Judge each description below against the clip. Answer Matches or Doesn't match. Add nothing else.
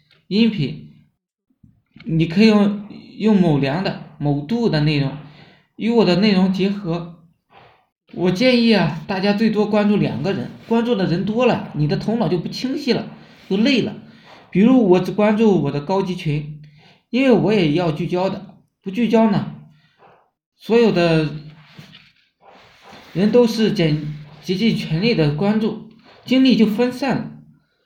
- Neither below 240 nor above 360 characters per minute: Doesn't match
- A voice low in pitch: Doesn't match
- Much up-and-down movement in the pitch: Doesn't match